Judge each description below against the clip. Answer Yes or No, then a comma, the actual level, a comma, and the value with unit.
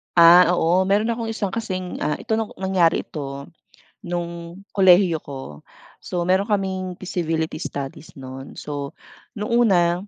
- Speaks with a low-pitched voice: No, medium, 175 Hz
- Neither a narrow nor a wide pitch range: Yes, average, 3.1 semitones